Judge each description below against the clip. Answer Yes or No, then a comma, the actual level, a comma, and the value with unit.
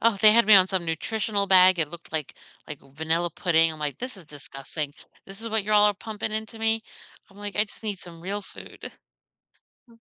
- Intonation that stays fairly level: No, average, 4.7 semitones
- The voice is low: No, high, 195 Hz